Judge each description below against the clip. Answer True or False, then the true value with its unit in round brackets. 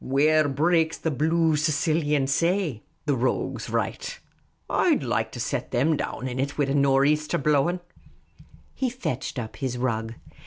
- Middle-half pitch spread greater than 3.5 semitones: False (3.0 semitones)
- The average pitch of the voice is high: False (145 Hz)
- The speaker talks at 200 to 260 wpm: False (160 wpm)